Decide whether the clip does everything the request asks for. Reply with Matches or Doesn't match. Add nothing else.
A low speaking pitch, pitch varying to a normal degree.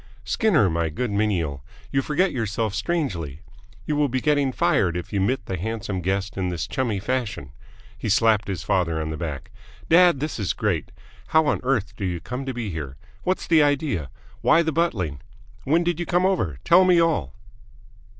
Doesn't match